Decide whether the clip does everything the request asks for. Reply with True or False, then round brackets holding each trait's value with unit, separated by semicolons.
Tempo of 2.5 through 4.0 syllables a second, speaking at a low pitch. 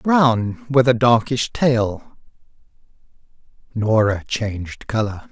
True (3.3 syllables/s; 120 Hz)